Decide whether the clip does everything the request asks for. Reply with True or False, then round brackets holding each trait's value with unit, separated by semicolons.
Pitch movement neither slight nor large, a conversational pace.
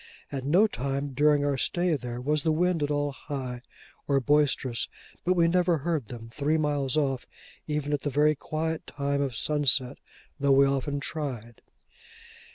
False (2.2 semitones; 165 wpm)